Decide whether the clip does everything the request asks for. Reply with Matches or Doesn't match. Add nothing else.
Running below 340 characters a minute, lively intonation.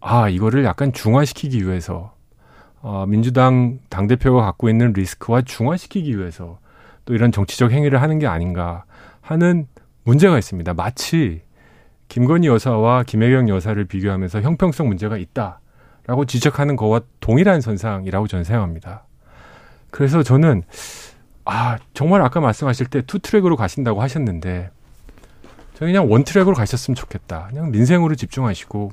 Doesn't match